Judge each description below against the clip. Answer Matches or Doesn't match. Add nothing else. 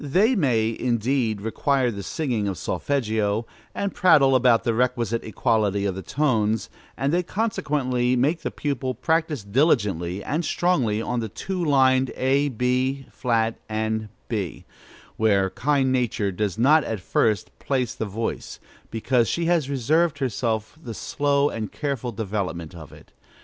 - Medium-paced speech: Matches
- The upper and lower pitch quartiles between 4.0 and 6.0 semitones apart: Matches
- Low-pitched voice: Matches